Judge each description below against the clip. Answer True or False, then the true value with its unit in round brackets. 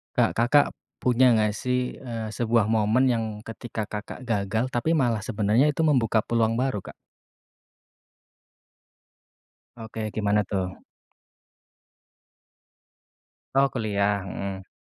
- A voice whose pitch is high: False (115 Hz)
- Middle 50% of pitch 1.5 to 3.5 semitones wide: True (3.1 semitones)